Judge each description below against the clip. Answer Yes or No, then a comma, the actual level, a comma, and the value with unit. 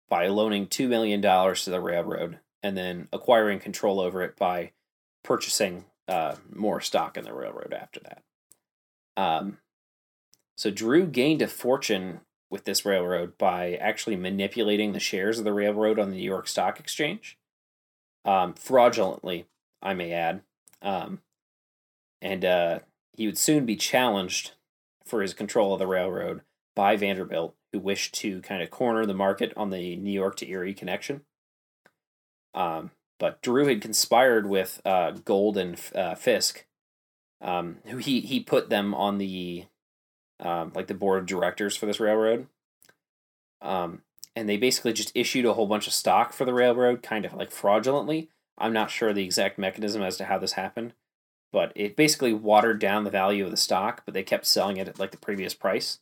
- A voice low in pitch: Yes, low, 100 Hz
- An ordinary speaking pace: Yes, average, 170 wpm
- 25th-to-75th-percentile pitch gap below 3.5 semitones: Yes, average, 3.0 semitones